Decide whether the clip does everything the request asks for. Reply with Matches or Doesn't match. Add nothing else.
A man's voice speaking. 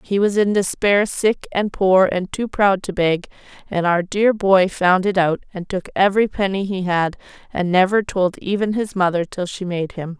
Doesn't match